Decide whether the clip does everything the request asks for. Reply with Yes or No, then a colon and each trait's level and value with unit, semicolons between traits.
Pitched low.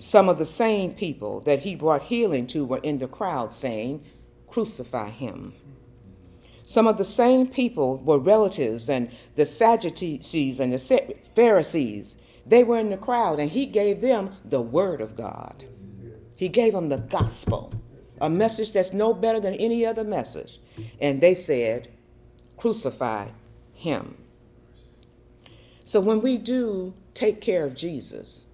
No: medium, 155 Hz